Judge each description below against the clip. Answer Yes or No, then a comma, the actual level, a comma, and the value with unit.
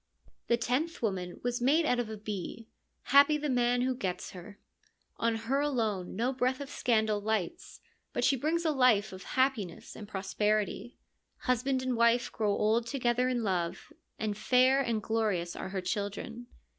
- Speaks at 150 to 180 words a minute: Yes, average, 170 wpm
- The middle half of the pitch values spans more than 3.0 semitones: Yes, average, 3.6 semitones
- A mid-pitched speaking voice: No, high, 235 Hz